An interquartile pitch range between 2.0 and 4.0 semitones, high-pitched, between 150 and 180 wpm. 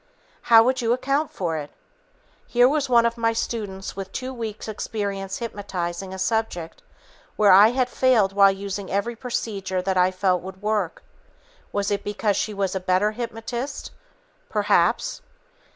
Yes: average, 3.5 semitones; high, 205 Hz; average, 155 wpm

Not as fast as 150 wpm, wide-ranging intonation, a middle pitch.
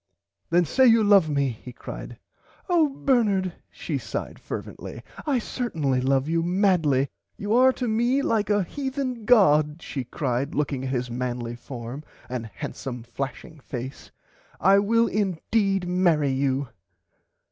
Yes: average, 140 wpm; wide, 8.5 semitones; medium, 165 Hz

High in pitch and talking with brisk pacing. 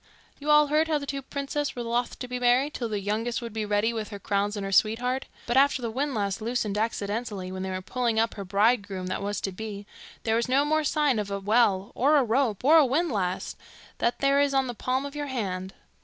Yes: high, 235 Hz; fast, 240 wpm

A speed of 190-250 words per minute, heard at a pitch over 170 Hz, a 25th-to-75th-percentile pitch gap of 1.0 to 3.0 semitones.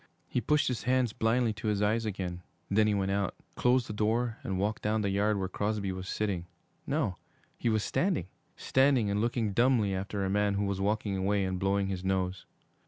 No: fast, 205 wpm; low, 105 Hz; narrow, 2.6 semitones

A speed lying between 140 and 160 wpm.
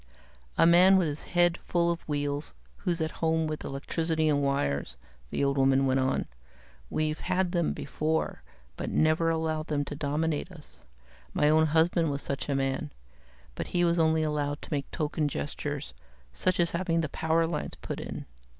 No: average, 175 wpm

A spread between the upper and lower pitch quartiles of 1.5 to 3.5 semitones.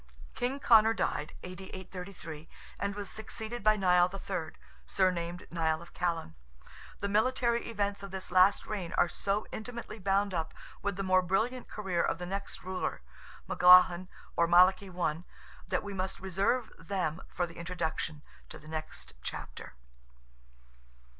Yes: average, 2.7 semitones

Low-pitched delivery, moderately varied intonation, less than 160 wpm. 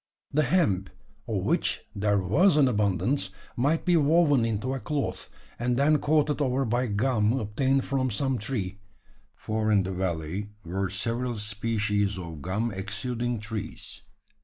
Yes: low, 110 Hz; average, 4.9 semitones; average, 145 wpm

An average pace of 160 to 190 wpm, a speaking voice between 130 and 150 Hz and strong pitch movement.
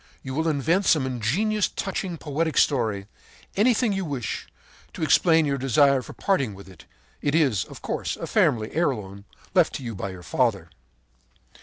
Yes: average, 165 wpm; medium, 140 Hz; wide, 7.0 semitones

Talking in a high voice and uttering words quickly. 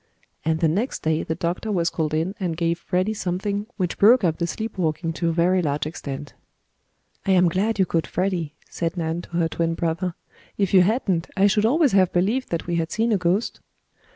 No: medium, 175 Hz; fast, 210 wpm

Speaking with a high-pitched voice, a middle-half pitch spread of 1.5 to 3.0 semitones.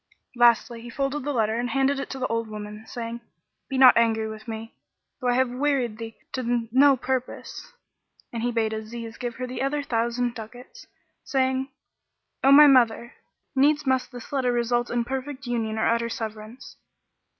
Yes: high, 240 Hz; narrow, 2.5 semitones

